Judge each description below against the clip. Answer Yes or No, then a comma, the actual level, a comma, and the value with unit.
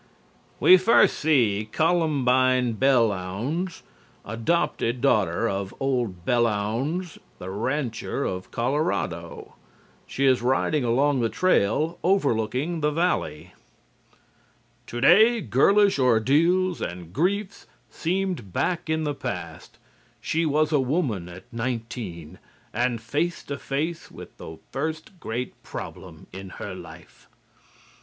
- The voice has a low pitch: Yes, low, 130 Hz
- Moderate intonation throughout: No, wide, 6.3 semitones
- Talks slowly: Yes, slow, 110 wpm